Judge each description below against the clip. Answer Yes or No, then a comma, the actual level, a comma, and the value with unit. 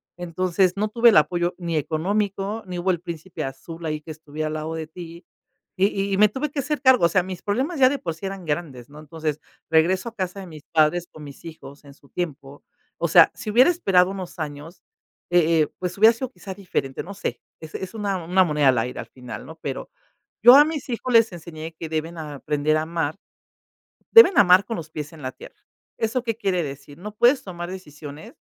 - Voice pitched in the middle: Yes, medium, 175 Hz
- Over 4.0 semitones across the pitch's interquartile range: Yes, average, 4.5 semitones